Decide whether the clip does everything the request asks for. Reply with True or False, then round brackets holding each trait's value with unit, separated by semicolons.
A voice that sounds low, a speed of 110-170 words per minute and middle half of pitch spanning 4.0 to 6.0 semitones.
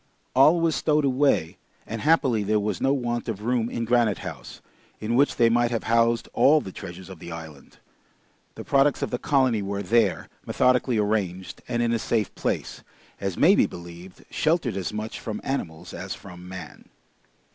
False (115 Hz; 180 wpm; 4.7 semitones)